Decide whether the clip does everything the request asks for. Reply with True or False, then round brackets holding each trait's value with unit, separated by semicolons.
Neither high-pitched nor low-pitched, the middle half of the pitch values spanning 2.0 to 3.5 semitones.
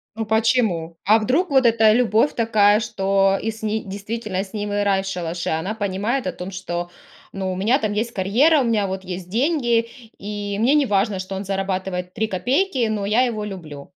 False (205 Hz; 3.2 semitones)